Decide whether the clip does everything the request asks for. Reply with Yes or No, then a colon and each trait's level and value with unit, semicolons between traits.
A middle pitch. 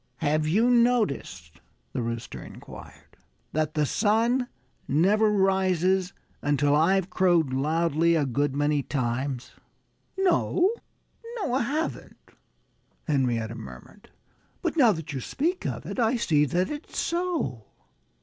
Yes: medium, 170 Hz